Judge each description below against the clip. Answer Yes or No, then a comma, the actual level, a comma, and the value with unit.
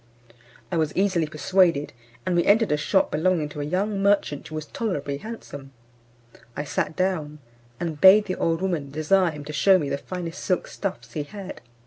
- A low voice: No, medium, 170 Hz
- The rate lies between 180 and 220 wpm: Yes, average, 185 wpm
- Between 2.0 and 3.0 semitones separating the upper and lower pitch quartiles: No, average, 4.3 semitones